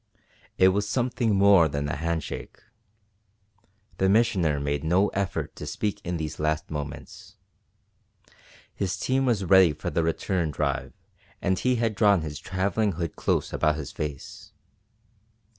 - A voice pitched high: No, very low, 90 Hz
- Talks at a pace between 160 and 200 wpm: No, average, 145 wpm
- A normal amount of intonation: Yes, average, 4.7 semitones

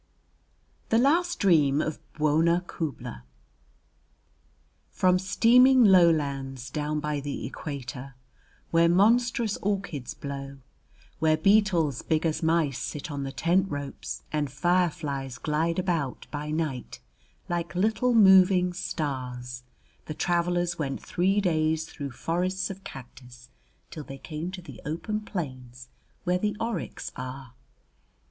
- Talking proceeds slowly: Yes, slow, 125 wpm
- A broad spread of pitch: No, average, 4.8 semitones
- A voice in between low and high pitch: Yes, medium, 160 Hz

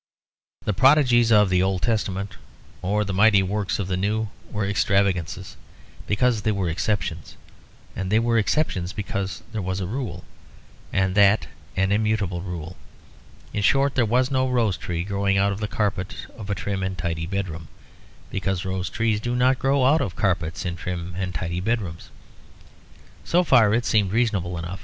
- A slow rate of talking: No, average, 170 wpm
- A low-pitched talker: Yes, low, 100 Hz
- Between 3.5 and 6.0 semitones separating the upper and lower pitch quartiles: No, average, 3.1 semitones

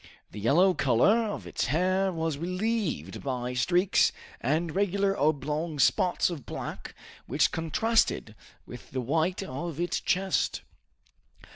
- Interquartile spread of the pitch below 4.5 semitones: No, average, 5.2 semitones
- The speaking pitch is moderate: Yes, medium, 165 Hz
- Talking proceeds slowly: Yes, slow, 125 wpm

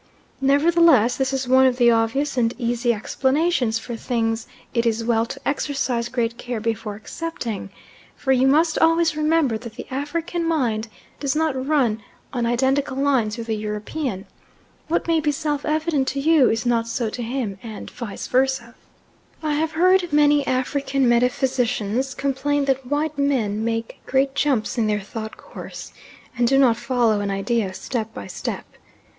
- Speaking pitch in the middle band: No, very high, 255 Hz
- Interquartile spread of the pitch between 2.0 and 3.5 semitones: No, average, 3.9 semitones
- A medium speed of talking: Yes, average, 165 wpm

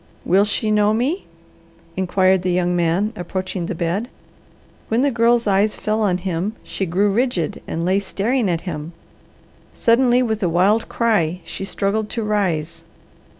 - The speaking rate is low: No, average, 155 wpm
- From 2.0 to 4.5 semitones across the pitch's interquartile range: Yes, average, 3.7 semitones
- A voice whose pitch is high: Yes, high, 195 Hz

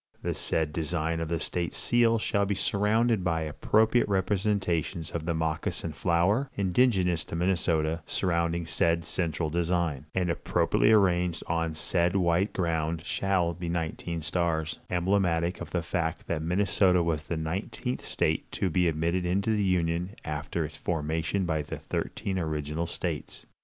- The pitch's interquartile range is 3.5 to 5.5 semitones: No, narrow, 2.6 semitones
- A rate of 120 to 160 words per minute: Yes, average, 150 wpm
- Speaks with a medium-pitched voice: No, very low, 85 Hz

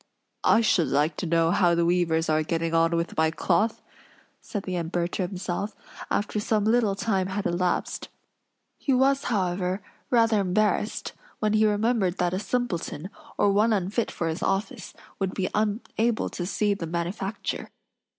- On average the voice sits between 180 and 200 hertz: Yes, high, 190 Hz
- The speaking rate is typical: Yes, average, 160 wpm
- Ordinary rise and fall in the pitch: Yes, average, 3.7 semitones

